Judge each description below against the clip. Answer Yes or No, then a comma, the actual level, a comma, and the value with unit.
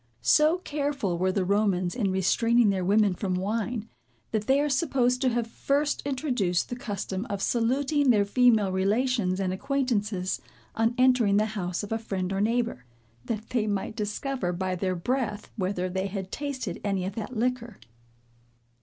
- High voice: Yes, high, 215 Hz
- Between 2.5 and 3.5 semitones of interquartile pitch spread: No, average, 4.7 semitones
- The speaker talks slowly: No, average, 165 wpm